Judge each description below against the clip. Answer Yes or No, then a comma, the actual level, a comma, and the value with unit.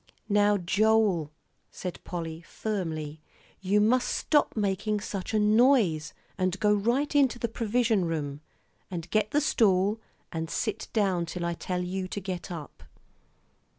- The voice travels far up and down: No, average, 4.0 semitones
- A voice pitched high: Yes, high, 195 Hz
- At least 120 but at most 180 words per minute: Yes, average, 150 wpm